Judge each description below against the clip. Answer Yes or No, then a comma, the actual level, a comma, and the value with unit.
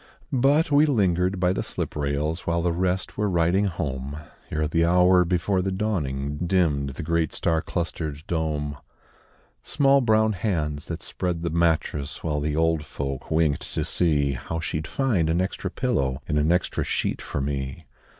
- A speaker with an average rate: Yes, average, 170 wpm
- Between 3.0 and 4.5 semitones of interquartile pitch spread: Yes, average, 3.8 semitones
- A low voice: Yes, very low, 85 Hz